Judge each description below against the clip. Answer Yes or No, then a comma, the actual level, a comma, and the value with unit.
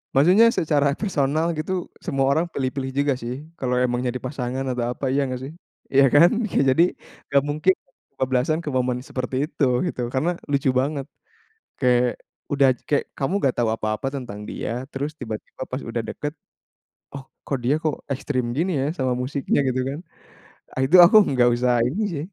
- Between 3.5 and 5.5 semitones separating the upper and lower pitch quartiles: No, average, 2.8 semitones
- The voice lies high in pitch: No, low, 135 Hz